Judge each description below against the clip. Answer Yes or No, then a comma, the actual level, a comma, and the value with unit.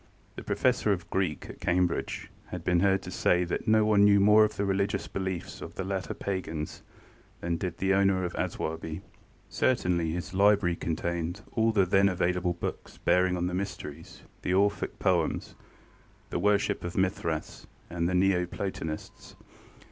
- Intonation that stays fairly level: Yes, narrow, 2.2 semitones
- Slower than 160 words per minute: No, average, 165 wpm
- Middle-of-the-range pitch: No, very low, 95 Hz